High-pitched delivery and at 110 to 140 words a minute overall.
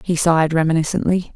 No: medium, 165 Hz; slow, 135 wpm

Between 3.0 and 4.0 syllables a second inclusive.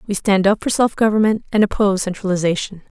No: 6.4 syllables/s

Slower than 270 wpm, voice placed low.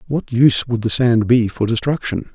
Yes: fast, 205 wpm; low, 120 Hz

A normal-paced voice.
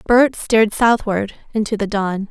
Yes: average, 155 wpm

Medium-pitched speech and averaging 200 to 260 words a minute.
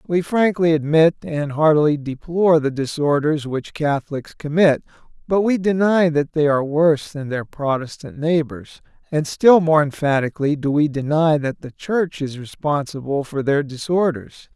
No: medium, 150 Hz; average, 155 wpm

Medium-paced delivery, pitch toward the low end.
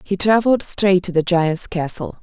No: average, 190 wpm; medium, 185 Hz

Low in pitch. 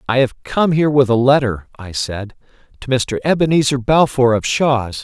Yes: low, 130 Hz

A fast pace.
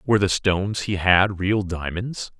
No: average, 175 wpm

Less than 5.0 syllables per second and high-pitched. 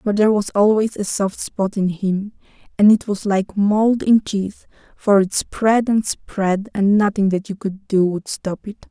Yes: 4.2 syllables/s; high, 205 Hz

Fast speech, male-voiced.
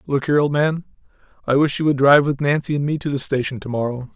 Yes: fast, 245 wpm; male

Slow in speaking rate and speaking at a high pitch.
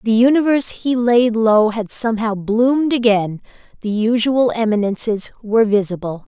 Yes: slow, 120 wpm; high, 225 Hz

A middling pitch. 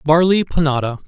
Yes: medium, 155 Hz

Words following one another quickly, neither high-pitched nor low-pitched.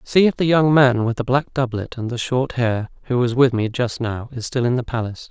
No: fast, 270 wpm; low, 125 Hz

